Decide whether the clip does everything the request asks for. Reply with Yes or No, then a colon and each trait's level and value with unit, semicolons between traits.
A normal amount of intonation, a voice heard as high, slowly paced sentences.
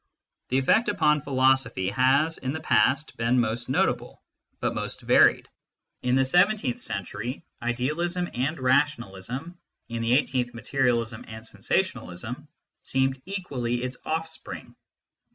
No: average, 4.2 semitones; low, 130 Hz; slow, 130 wpm